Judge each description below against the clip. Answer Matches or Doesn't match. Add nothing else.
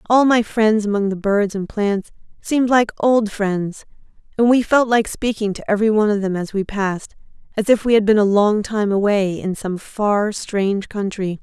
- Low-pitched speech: Doesn't match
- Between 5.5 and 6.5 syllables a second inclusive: Doesn't match